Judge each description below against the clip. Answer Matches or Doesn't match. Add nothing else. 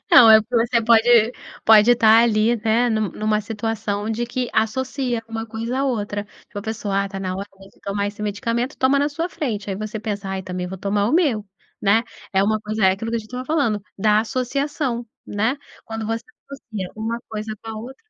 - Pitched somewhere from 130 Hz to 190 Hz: Doesn't match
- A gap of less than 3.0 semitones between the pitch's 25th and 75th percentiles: Matches